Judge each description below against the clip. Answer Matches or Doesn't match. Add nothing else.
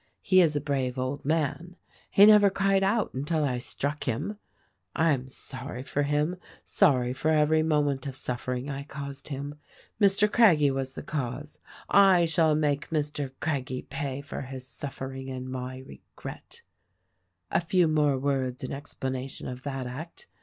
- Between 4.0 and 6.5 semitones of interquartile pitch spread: Doesn't match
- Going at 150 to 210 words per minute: Matches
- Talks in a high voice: Doesn't match